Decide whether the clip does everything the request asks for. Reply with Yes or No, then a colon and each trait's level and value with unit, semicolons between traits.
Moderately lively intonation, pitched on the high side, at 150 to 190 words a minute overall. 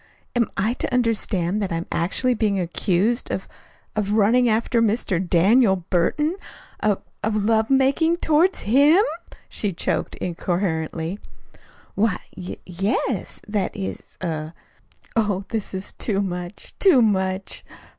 No: average, 4.3 semitones; high, 205 Hz; slow, 135 wpm